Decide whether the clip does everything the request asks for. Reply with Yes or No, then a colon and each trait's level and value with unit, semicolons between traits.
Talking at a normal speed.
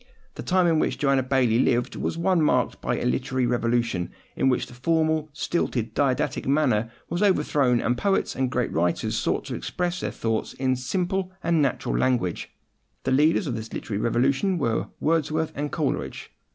Yes: average, 180 wpm